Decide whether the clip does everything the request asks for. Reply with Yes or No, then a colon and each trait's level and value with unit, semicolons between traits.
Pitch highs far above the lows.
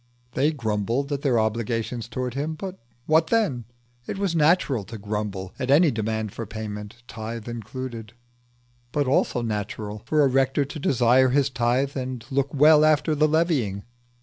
No: average, 4.7 semitones